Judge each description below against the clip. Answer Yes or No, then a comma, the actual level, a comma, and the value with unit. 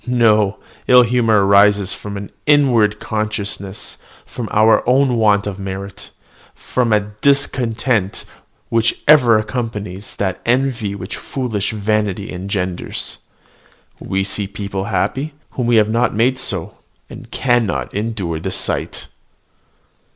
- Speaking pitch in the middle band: No, low, 105 Hz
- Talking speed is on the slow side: Yes, slow, 120 wpm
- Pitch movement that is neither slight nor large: Yes, average, 3.2 semitones